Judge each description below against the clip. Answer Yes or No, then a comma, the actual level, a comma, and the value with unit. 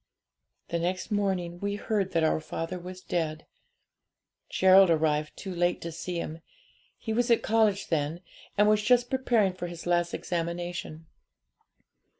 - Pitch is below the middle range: No, medium, 175 Hz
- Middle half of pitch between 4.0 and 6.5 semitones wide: No, average, 3.4 semitones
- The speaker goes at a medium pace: Yes, average, 150 wpm